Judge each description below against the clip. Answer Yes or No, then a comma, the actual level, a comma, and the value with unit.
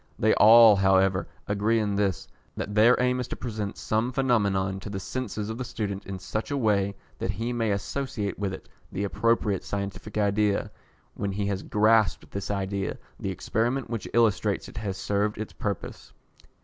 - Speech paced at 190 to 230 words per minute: No, average, 175 wpm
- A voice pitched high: No, low, 105 Hz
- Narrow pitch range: Yes, narrow, 2.3 semitones